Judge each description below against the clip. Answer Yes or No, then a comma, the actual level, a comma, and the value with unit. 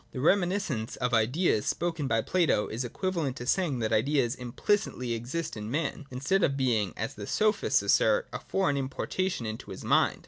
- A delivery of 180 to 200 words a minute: Yes, average, 185 wpm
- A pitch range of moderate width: No, wide, 7.0 semitones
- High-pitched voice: No, low, 135 Hz